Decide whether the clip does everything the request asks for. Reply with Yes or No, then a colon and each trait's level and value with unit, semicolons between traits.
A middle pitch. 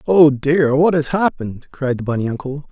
Yes: medium, 145 Hz